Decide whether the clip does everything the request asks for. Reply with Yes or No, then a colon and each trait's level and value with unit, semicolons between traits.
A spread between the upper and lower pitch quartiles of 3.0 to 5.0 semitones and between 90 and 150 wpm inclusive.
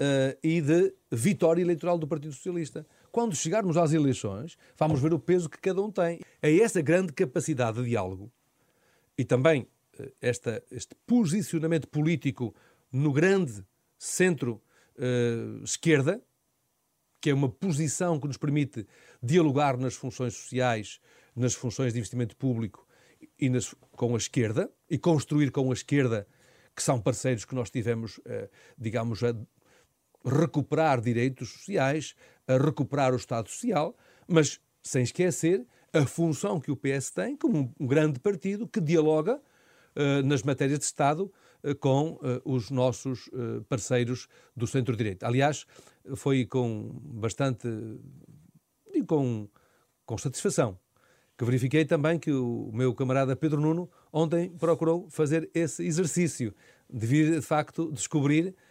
Yes: average, 4.7 semitones; average, 140 wpm